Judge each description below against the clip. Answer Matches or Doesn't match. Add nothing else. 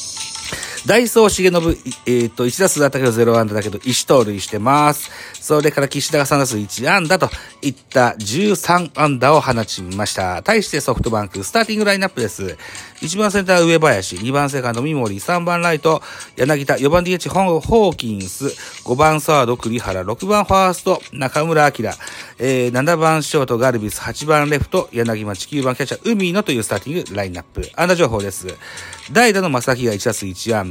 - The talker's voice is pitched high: Doesn't match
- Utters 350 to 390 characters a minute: Matches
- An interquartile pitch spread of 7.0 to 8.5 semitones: Doesn't match